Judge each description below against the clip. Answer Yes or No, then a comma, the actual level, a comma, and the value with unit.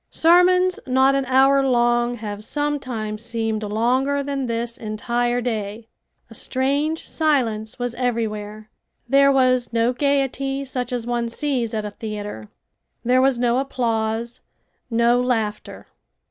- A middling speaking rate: No, slow, 130 wpm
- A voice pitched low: No, high, 245 Hz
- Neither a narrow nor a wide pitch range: Yes, average, 3.2 semitones